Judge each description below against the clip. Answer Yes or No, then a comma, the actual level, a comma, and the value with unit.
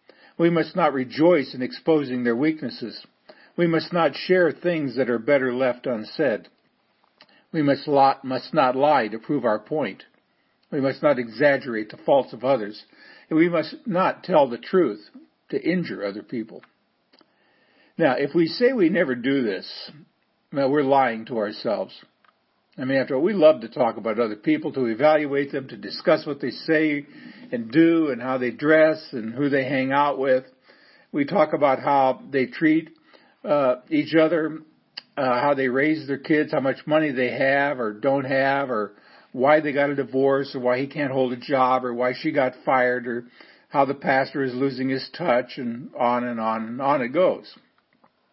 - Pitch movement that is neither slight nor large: Yes, average, 3.6 semitones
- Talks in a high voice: No, medium, 140 Hz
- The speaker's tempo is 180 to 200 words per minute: Yes, average, 185 wpm